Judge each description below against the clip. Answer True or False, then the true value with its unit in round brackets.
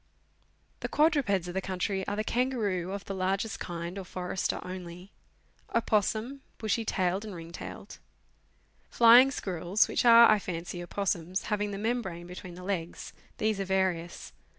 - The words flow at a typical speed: True (150 wpm)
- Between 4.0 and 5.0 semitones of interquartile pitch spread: False (3.3 semitones)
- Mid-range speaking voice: False (195 Hz)